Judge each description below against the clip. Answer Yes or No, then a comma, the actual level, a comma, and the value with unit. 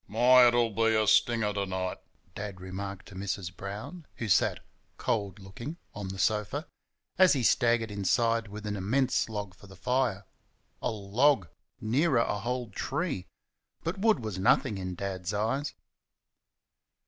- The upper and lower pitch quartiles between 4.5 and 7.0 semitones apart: No, average, 3.8 semitones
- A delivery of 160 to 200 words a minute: No, average, 150 wpm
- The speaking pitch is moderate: No, low, 105 Hz